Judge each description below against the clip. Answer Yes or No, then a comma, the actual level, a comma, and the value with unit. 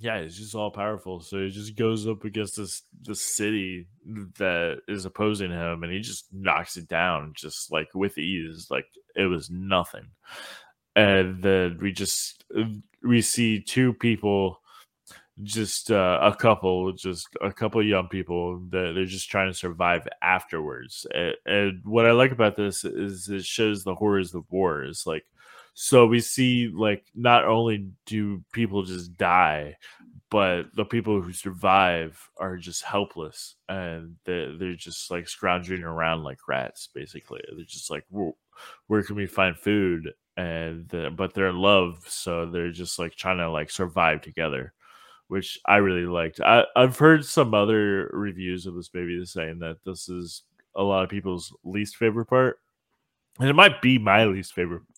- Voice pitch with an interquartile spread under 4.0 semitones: Yes, average, 3.2 semitones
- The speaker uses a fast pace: No, average, 170 wpm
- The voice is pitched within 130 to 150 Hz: No, very low, 95 Hz